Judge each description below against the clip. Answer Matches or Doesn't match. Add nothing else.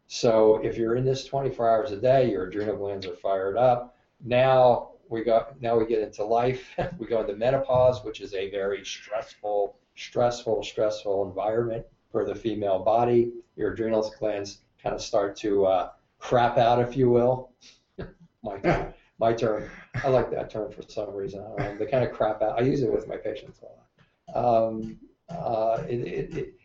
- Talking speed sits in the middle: Matches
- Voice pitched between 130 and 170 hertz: Doesn't match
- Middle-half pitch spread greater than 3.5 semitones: Doesn't match